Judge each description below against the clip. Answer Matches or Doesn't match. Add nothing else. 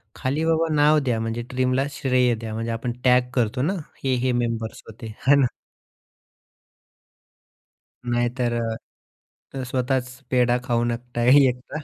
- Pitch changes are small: Matches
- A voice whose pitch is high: Doesn't match